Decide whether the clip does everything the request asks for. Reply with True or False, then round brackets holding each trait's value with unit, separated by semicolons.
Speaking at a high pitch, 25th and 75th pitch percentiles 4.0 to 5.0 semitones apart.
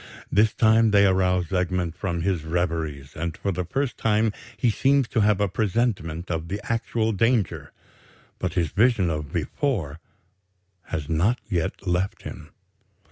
False (95 Hz; 4.7 semitones)